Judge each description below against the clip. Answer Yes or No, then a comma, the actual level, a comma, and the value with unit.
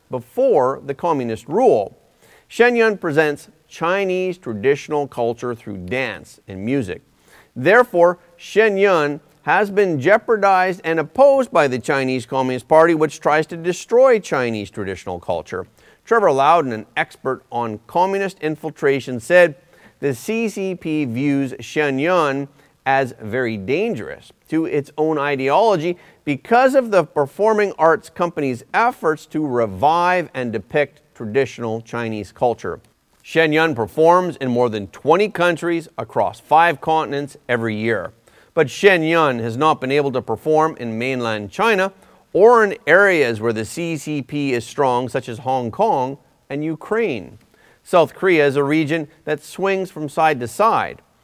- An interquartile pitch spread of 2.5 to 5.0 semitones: No, wide, 5.5 semitones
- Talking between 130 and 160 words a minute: Yes, average, 140 wpm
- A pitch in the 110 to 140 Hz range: No, medium, 150 Hz